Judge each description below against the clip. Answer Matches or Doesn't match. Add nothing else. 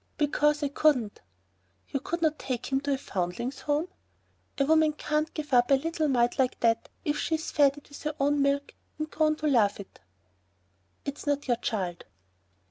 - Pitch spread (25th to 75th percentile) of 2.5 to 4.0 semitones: Matches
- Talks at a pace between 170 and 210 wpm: Matches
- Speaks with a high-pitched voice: Matches